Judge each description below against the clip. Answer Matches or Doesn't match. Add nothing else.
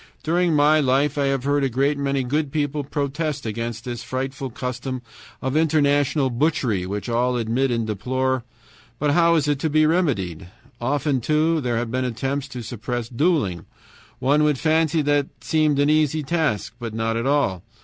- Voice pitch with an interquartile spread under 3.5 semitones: Doesn't match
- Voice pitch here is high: Doesn't match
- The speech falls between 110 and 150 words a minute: Doesn't match